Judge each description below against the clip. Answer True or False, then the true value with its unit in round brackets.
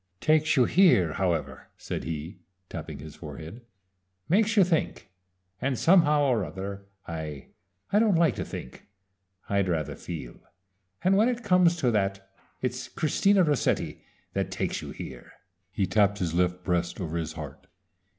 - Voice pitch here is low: True (100 Hz)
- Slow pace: False (150 wpm)